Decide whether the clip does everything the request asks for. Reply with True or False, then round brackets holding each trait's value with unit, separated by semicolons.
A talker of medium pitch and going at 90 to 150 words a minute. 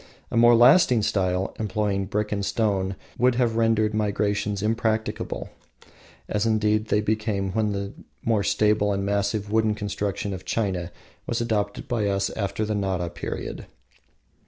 False (105 Hz; 145 wpm)